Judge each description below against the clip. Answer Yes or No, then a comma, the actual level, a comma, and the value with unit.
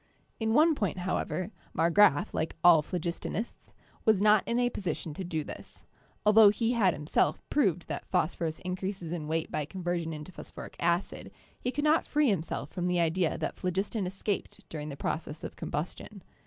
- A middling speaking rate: Yes, average, 175 wpm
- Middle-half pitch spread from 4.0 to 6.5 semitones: Yes, average, 4.4 semitones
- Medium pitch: Yes, medium, 180 Hz